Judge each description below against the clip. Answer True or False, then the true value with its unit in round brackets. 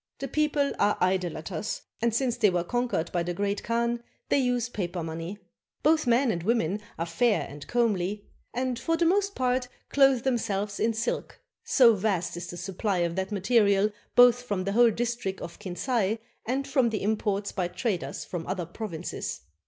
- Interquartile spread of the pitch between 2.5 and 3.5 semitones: False (5.0 semitones)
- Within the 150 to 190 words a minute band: True (180 wpm)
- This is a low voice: False (215 Hz)